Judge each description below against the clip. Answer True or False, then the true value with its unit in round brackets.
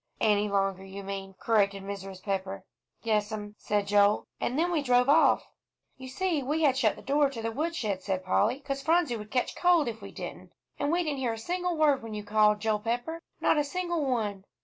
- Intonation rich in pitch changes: True (6.1 semitones)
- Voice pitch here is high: True (230 Hz)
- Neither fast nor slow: False (215 wpm)